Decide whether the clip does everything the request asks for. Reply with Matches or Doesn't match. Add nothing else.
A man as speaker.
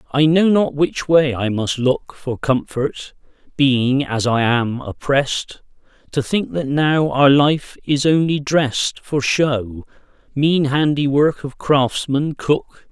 Matches